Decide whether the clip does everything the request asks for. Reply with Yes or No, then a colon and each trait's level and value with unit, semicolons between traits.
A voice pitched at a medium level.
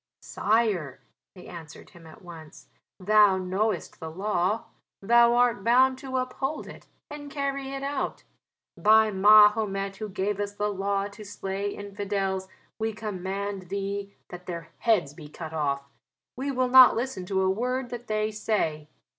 No: high, 205 Hz